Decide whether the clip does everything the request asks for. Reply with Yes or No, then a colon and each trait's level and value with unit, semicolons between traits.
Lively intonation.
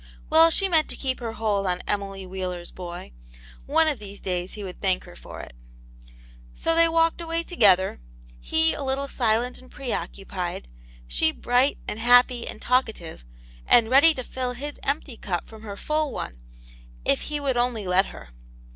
Yes: wide, 6.8 semitones